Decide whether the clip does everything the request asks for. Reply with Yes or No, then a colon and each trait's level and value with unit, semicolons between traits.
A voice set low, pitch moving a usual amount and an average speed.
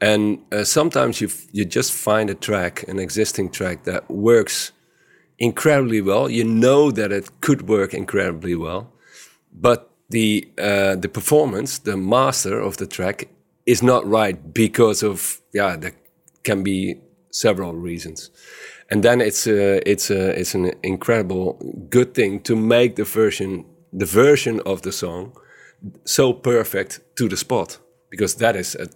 Yes: low, 105 Hz; average, 3.5 semitones; average, 155 wpm